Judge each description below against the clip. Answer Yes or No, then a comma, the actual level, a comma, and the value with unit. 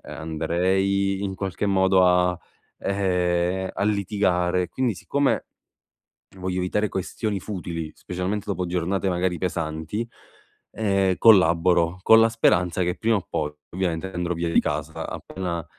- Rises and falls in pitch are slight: Yes, narrow, 1.9 semitones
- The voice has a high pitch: No, very low, 90 Hz